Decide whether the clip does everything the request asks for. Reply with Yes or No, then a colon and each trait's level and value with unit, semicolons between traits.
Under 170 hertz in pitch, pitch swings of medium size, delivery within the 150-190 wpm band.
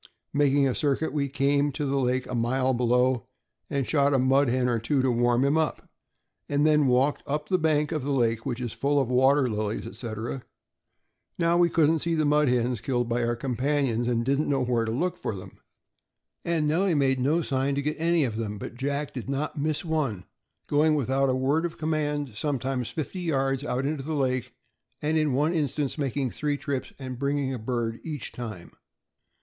No: low, 135 Hz; average, 3.1 semitones; fast, 205 wpm